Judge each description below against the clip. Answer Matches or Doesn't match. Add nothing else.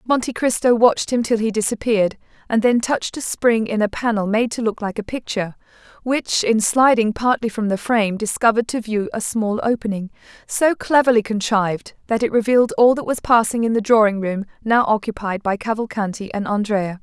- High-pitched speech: Matches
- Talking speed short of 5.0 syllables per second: Doesn't match